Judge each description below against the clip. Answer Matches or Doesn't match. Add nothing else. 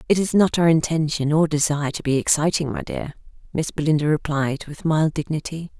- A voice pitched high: Doesn't match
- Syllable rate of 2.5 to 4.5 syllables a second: Doesn't match